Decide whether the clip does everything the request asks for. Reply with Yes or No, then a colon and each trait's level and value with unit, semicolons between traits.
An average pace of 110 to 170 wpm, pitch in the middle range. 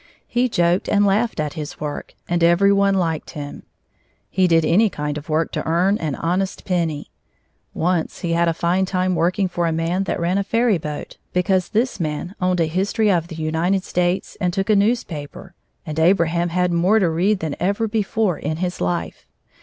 No: average, 195 wpm; medium, 175 Hz